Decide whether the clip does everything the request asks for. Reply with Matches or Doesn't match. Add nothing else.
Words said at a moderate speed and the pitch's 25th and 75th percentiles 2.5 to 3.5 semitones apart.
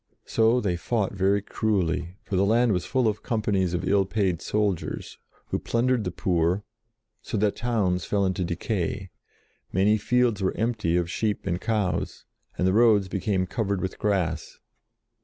Matches